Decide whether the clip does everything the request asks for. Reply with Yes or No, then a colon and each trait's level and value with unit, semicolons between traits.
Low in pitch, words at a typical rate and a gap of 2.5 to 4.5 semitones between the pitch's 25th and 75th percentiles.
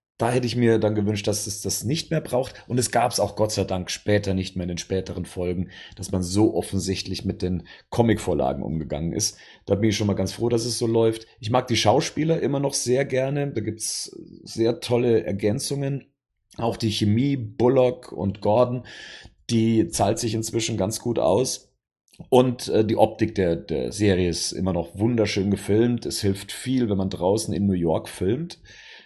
No: low, 110 Hz; fast, 200 wpm; average, 3.8 semitones